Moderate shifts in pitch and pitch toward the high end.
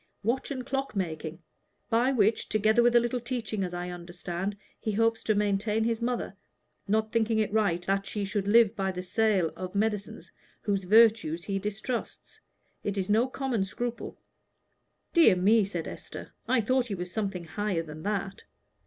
Yes: average, 3.2 semitones; high, 210 Hz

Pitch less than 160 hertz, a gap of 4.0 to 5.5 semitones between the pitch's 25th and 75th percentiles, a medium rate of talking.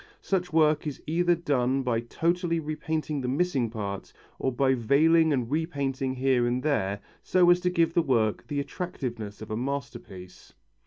Yes: medium, 140 Hz; average, 5.1 semitones; average, 165 wpm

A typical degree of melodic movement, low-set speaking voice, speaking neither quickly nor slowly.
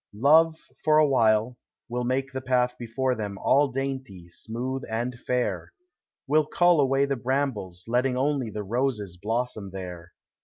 Yes: average, 4.0 semitones; low, 125 Hz; average, 155 wpm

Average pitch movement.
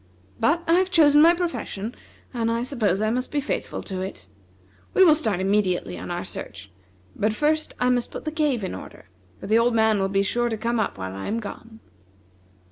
No: wide, 6.9 semitones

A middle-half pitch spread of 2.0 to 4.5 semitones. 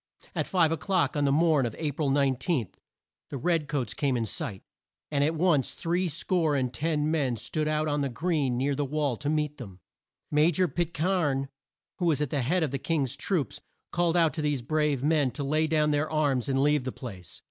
Yes: average, 2.9 semitones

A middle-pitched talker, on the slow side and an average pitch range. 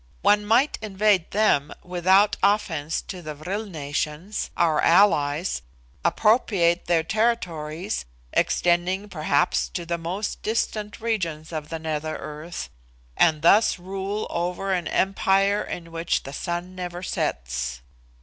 Yes: medium, 175 Hz; slow, 125 wpm; average, 4.2 semitones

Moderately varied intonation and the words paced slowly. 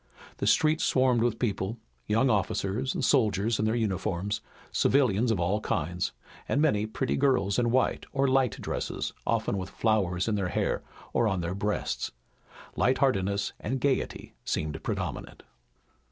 No: average, 4.8 semitones; average, 155 wpm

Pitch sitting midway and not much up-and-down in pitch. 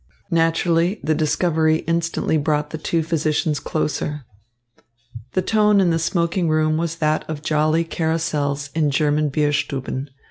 Yes: medium, 155 Hz; narrow, 1.9 semitones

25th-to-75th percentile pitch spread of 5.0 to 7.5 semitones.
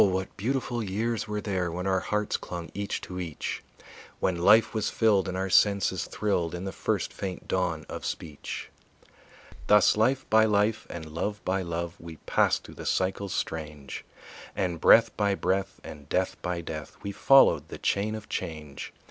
No: average, 3.6 semitones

